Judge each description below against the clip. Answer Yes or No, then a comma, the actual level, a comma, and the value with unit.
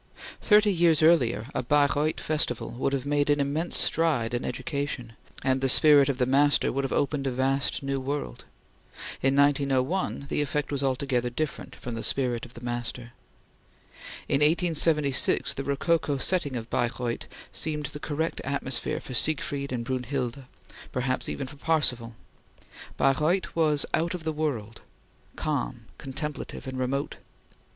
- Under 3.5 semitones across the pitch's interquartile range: Yes, average, 2.9 semitones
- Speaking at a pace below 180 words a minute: Yes, average, 150 wpm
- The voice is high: No, medium, 140 Hz